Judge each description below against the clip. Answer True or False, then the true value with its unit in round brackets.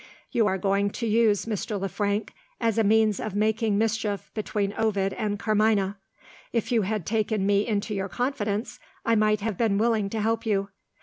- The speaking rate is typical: True (185 wpm)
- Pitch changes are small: True (1.8 semitones)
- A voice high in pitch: True (215 Hz)